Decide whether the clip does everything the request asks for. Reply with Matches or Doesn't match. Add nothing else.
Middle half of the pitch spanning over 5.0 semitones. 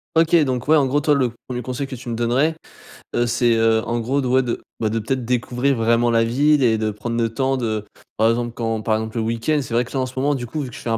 Doesn't match